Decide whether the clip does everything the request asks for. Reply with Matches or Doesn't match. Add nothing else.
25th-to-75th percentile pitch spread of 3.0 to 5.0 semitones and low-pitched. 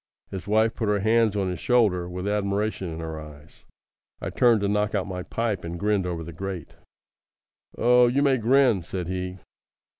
Matches